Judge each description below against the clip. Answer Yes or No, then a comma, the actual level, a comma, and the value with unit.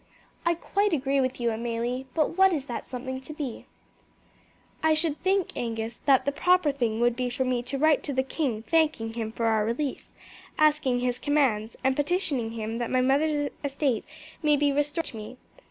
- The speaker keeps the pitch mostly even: No, average, 4.1 semitones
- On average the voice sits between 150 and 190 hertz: No, very high, 265 Hz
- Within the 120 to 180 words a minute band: No, average, 190 wpm